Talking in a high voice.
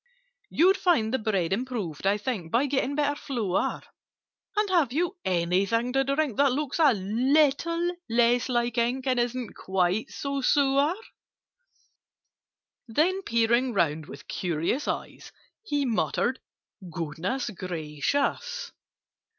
Yes: high, 245 Hz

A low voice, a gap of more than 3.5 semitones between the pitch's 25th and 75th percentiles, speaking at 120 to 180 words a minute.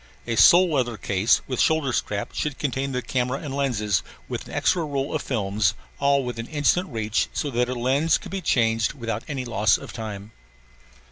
No: low, 125 Hz; average, 4.0 semitones; average, 190 wpm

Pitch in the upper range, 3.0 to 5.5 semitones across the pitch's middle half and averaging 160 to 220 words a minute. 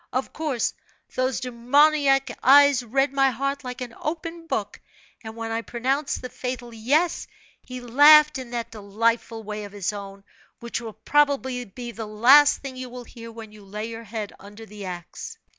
Yes: high, 245 Hz; average, 3.5 semitones; average, 175 wpm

